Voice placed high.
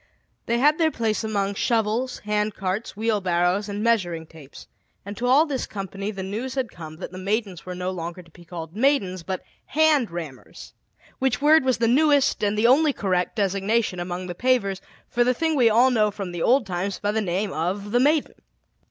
Yes: high, 210 Hz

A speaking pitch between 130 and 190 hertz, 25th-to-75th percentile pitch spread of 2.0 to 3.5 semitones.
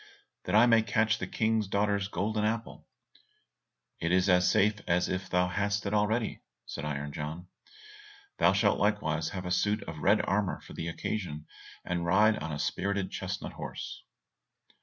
No: low, 100 Hz; average, 3.2 semitones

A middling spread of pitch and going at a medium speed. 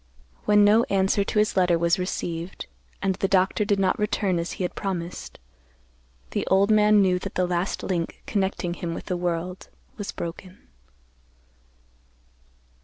No: narrow, 2.3 semitones; average, 155 wpm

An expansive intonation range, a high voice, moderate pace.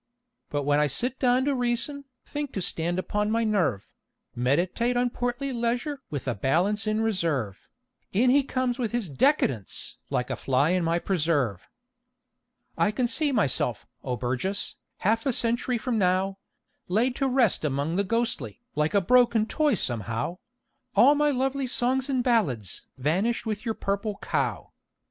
Yes: wide, 7.8 semitones; high, 215 Hz; average, 160 wpm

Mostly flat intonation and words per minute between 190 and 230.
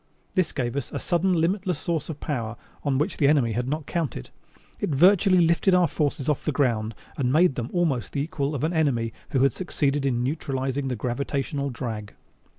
No: average, 4.4 semitones; average, 195 wpm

